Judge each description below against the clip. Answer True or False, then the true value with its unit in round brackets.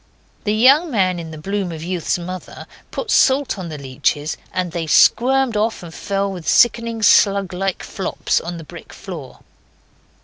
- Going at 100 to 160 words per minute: False (170 wpm)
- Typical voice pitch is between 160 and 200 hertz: True (190 Hz)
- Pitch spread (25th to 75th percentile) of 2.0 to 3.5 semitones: False (4.6 semitones)